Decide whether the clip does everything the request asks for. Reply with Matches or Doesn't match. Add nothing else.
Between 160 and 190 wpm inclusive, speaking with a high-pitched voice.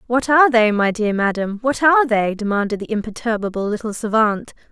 Matches